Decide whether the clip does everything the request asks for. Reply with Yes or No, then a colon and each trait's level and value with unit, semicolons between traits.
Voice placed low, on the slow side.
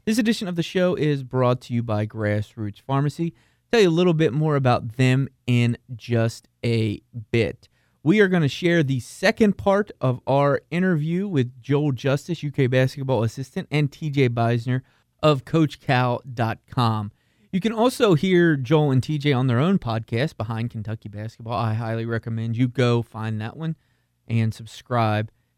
No: low, 130 Hz; average, 165 wpm